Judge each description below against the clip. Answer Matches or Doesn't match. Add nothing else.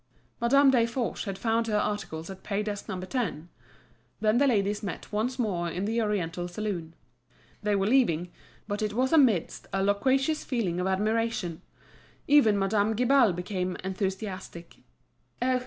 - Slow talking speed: Doesn't match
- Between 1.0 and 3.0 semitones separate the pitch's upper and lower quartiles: Doesn't match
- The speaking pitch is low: Doesn't match